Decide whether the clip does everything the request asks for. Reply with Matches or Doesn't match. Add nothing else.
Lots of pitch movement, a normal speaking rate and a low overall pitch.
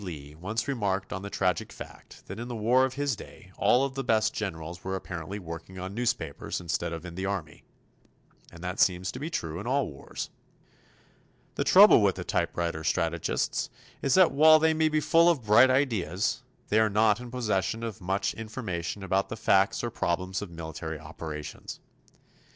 Matches